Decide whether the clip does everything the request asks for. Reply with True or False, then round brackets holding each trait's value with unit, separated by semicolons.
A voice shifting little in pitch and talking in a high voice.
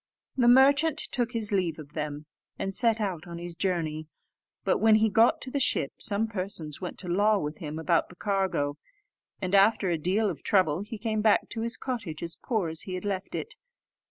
False (4.9 semitones; 195 Hz)